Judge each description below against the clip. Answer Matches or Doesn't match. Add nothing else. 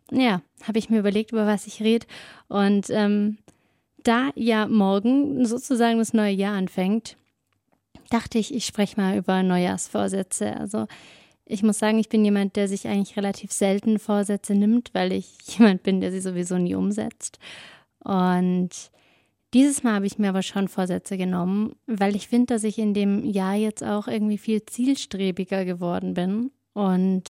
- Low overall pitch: Doesn't match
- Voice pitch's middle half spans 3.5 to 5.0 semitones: Doesn't match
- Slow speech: Doesn't match